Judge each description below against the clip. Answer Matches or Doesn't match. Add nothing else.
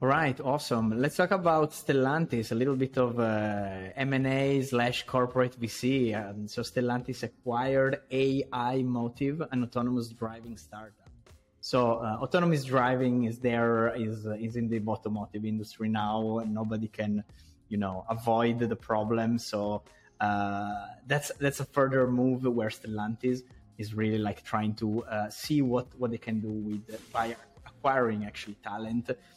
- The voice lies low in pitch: Matches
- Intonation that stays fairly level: Doesn't match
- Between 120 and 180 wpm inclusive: Matches